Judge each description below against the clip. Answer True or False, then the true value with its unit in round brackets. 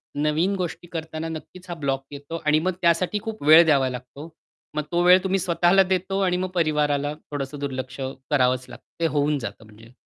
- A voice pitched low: False (155 Hz)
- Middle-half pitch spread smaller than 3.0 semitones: False (4.0 semitones)